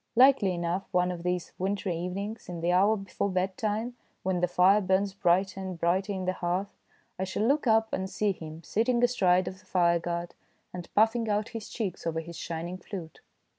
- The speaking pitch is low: No, high, 190 Hz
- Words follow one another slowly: No, average, 190 wpm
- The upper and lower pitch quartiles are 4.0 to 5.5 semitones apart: No, average, 2.8 semitones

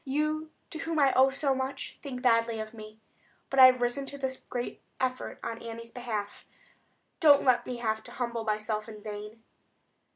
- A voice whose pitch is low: No, high, 245 Hz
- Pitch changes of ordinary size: Yes, average, 3.3 semitones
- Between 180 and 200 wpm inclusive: Yes, average, 185 wpm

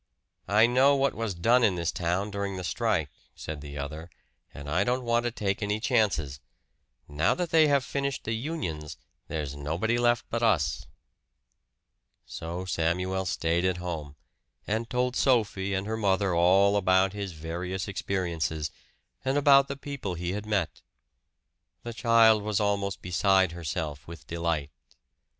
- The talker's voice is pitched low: Yes, very low, 95 Hz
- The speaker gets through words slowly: No, average, 155 wpm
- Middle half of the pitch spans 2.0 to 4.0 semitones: No, average, 5.3 semitones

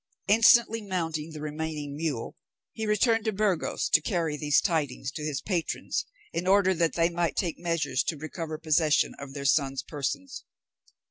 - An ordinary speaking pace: Yes, average, 160 wpm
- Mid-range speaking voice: Yes, medium, 160 Hz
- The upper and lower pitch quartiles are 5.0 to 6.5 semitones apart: No, average, 4.0 semitones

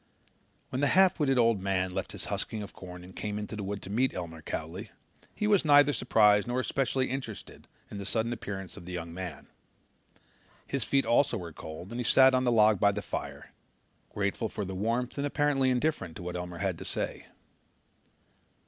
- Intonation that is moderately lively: No, wide, 5.7 semitones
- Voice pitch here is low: Yes, low, 105 Hz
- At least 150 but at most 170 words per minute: No, average, 200 wpm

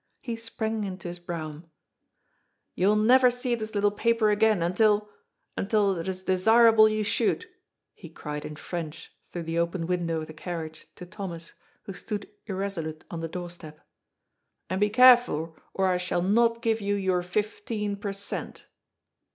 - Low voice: No, high, 195 Hz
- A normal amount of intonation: Yes, average, 4.1 semitones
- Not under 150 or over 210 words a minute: Yes, average, 175 wpm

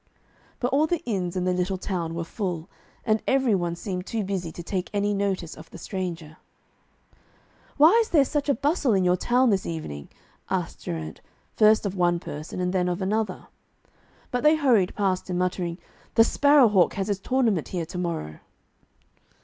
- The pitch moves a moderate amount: Yes, average, 4.5 semitones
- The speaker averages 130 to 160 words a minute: No, average, 180 wpm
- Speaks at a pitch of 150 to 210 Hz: Yes, high, 190 Hz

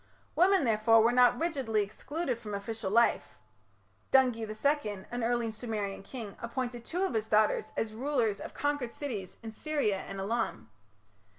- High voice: Yes, high, 230 Hz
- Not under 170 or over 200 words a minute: No, average, 155 wpm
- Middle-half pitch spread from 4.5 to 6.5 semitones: No, average, 3.5 semitones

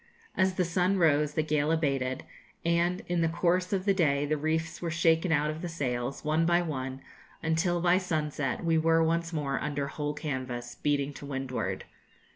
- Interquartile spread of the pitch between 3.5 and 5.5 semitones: No, average, 3.1 semitones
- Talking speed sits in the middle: Yes, average, 185 wpm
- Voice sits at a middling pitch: Yes, medium, 155 Hz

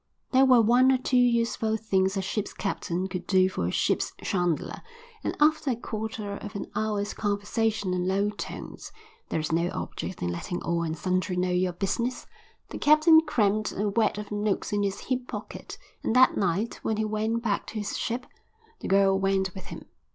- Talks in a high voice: Yes, high, 205 Hz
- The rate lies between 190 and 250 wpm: Yes, average, 195 wpm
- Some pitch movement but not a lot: Yes, average, 3.4 semitones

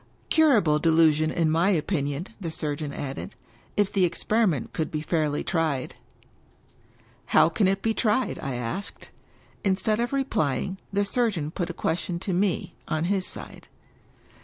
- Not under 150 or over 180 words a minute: Yes, average, 160 wpm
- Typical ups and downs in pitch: Yes, average, 4.7 semitones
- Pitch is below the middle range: No, medium, 170 Hz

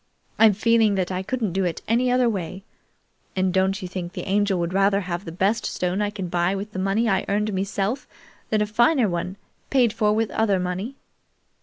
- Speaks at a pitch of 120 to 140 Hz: No, high, 200 Hz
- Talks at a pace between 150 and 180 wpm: No, average, 200 wpm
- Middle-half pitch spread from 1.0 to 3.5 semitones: Yes, average, 2.8 semitones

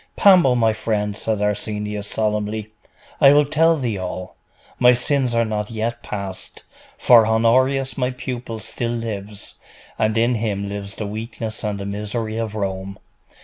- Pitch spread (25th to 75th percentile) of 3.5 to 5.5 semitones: No, narrow, 2.6 semitones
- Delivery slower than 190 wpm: Yes, average, 150 wpm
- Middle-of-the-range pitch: No, low, 110 Hz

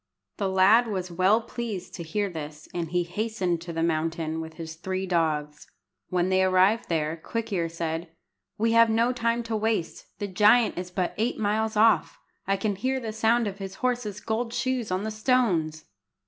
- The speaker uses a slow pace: No, average, 185 wpm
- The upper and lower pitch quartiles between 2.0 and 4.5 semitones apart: No, average, 4.9 semitones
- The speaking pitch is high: Yes, high, 195 Hz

